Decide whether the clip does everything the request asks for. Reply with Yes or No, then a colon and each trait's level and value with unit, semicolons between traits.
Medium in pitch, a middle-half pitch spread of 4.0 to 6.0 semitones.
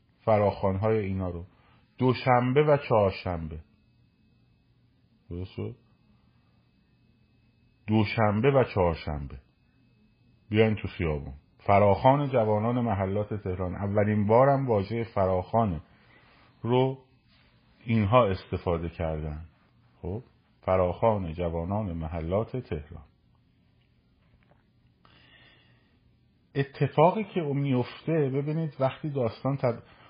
No: low, 110 Hz; average, 5.1 semitones